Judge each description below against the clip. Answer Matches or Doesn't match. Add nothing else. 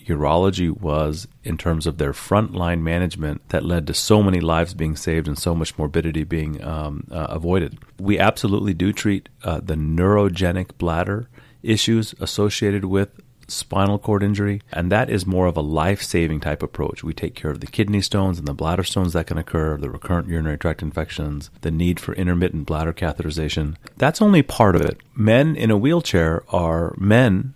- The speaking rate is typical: Matches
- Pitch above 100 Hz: Doesn't match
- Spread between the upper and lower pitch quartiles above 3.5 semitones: Matches